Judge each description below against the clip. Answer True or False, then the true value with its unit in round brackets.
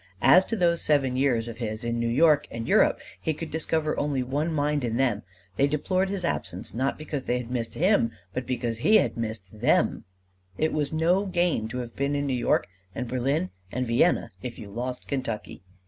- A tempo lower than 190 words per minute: False (205 wpm)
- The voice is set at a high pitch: False (135 Hz)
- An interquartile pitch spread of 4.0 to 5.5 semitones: True (4.9 semitones)